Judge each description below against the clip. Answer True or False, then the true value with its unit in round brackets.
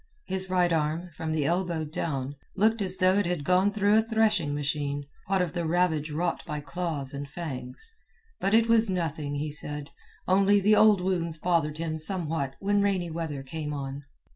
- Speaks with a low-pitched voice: False (170 Hz)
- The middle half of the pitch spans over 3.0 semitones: True (4.3 semitones)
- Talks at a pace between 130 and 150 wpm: False (185 wpm)